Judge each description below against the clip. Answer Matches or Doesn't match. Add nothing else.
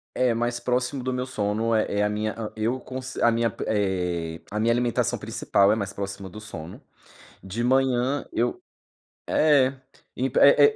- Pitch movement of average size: Matches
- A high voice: Doesn't match